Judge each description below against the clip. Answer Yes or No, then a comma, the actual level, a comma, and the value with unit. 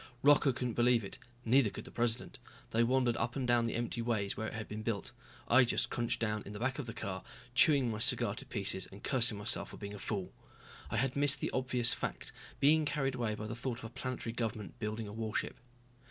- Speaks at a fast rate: Yes, fast, 230 wpm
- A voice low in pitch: Yes, low, 115 Hz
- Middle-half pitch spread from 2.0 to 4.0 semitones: Yes, average, 2.9 semitones